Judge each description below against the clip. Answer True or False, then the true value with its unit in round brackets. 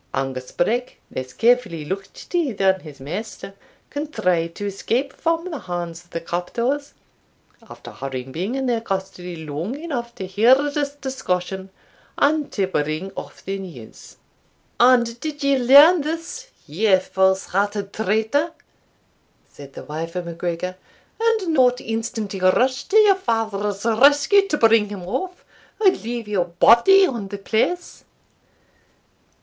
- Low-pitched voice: False (215 Hz)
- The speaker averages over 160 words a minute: False (140 wpm)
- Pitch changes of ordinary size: False (7.4 semitones)